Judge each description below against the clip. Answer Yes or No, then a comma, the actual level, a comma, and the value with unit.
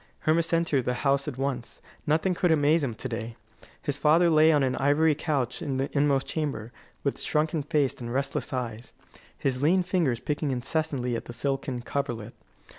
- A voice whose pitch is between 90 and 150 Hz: Yes, medium, 140 Hz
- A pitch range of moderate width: Yes, average, 3.6 semitones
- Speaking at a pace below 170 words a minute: No, average, 180 wpm